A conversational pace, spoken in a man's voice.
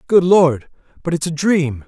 Yes: average, 190 wpm; male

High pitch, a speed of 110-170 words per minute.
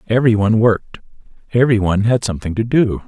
No: low, 110 Hz; slow, 135 wpm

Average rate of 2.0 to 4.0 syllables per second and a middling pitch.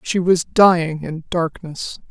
Yes: 3.7 syllables/s; medium, 170 Hz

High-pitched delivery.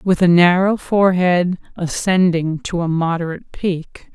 No: medium, 180 Hz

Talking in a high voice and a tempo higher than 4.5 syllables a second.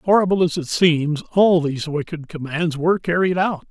No: medium, 165 Hz; 5.1 syllables/s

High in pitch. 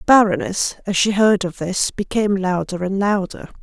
Yes: high, 195 Hz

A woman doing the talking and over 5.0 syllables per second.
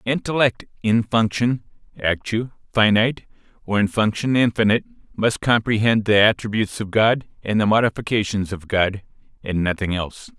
No: male; 5.4 syllables/s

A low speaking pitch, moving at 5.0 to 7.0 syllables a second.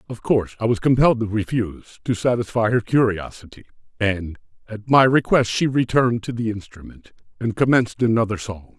Yes: low, 110 Hz; 5.8 syllables/s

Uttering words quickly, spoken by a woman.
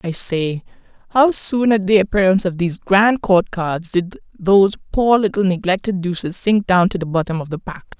No: average, 195 wpm; female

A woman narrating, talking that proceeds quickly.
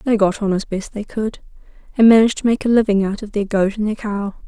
Yes: female; fast, 270 wpm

